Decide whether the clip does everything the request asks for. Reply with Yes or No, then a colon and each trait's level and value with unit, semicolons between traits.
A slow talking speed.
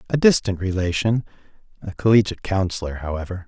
Yes: slow, 105 wpm